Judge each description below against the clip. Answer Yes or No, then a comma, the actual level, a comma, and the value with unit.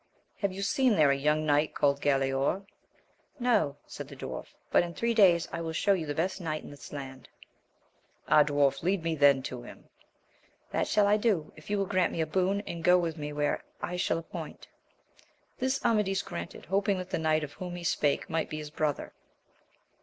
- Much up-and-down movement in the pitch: No, average, 4.7 semitones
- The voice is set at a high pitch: No, medium, 165 Hz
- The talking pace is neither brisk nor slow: No, fast, 215 wpm